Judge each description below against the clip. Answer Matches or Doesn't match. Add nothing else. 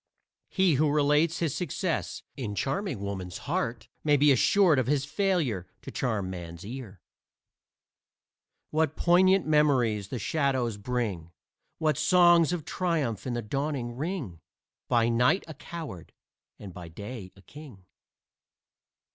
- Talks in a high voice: Doesn't match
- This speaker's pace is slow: Matches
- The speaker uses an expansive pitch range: Matches